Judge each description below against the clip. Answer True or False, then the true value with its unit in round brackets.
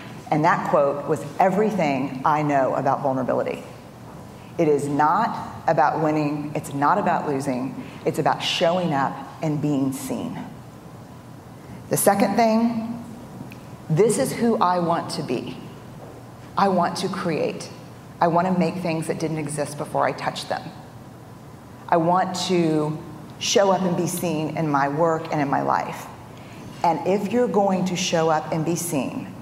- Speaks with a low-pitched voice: False (165 Hz)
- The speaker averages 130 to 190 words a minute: True (155 wpm)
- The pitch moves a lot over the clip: False (3.4 semitones)